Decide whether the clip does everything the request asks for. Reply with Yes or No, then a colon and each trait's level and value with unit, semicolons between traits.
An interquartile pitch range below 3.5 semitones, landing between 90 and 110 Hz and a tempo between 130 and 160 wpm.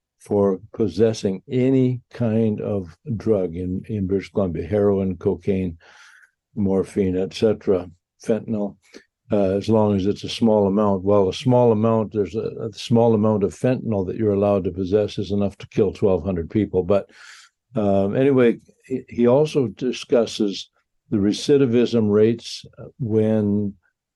Yes: narrow, 2.6 semitones; low, 105 Hz; average, 140 wpm